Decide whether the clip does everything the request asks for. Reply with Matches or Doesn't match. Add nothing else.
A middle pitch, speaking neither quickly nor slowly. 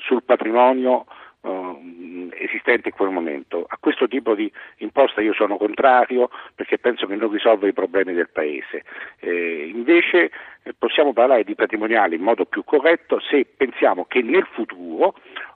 Doesn't match